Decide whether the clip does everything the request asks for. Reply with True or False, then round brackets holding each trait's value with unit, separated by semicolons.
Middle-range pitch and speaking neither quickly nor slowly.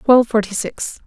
False (225 Hz; 170 wpm)